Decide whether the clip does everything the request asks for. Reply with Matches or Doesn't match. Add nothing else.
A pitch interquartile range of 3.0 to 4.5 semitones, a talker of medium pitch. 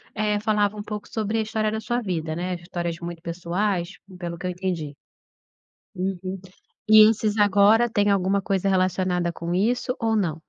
Doesn't match